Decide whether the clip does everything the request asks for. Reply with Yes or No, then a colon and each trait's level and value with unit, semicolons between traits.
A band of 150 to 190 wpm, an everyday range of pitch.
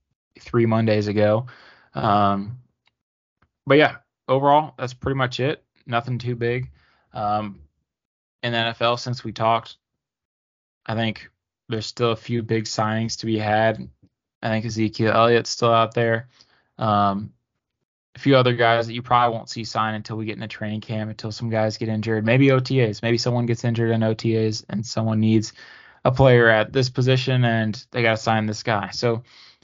No: average, 170 wpm; narrow, 1.9 semitones